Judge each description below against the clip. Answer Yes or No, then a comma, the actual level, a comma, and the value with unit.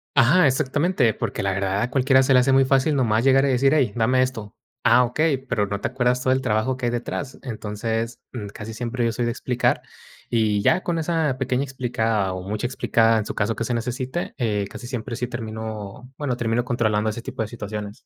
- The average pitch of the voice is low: Yes, low, 120 Hz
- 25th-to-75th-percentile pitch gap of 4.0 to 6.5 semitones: No, average, 3.1 semitones